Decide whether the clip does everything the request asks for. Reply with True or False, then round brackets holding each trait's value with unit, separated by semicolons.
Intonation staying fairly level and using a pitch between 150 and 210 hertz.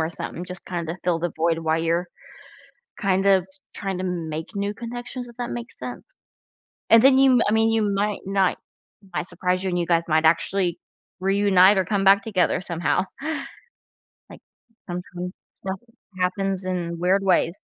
True (2.3 semitones; 185 Hz)